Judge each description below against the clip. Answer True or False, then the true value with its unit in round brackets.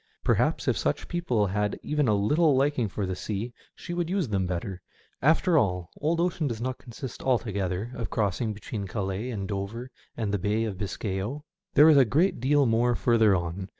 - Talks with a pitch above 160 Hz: False (115 Hz)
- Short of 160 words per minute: False (195 wpm)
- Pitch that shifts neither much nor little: False (5.9 semitones)